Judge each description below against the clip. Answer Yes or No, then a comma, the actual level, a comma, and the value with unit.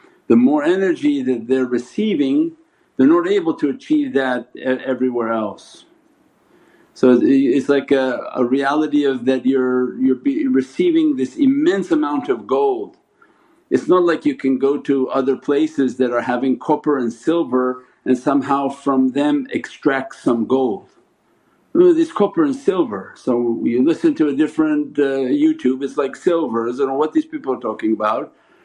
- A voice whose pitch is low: No, medium, 145 Hz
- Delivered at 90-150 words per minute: No, average, 160 wpm